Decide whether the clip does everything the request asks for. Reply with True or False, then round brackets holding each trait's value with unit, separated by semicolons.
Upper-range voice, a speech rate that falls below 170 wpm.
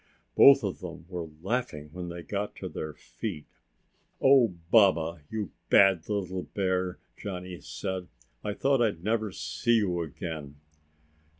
False (95 Hz; 135 wpm)